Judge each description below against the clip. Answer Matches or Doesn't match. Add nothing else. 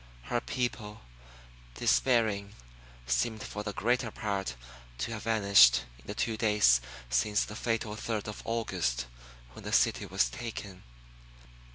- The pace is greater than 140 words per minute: Doesn't match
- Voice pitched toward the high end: Doesn't match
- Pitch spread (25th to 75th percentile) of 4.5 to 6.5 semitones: Doesn't match